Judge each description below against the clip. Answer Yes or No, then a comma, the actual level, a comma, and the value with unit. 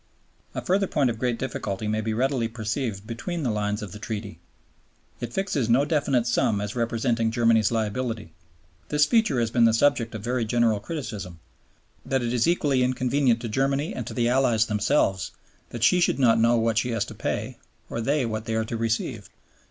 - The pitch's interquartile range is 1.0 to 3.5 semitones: Yes, average, 2.8 semitones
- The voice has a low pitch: Yes, low, 115 Hz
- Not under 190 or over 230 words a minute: Yes, average, 195 wpm